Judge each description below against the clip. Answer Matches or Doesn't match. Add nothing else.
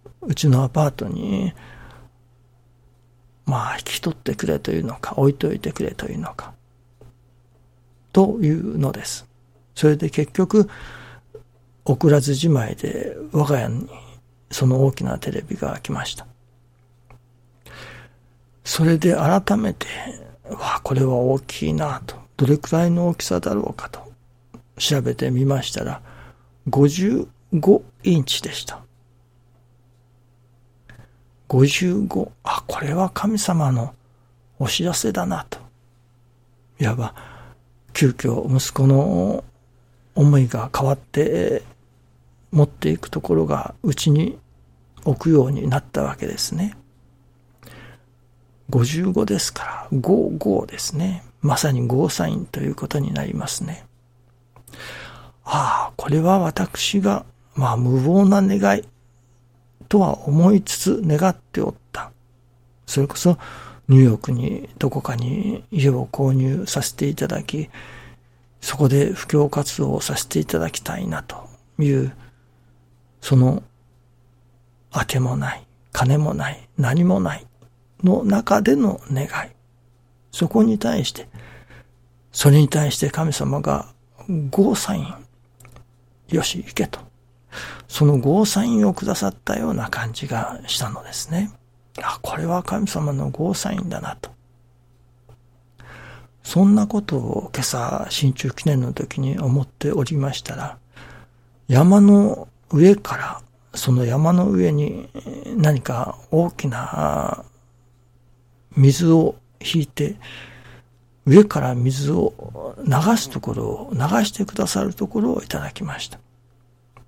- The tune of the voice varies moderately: Matches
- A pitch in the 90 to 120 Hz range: Doesn't match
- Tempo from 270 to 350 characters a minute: Doesn't match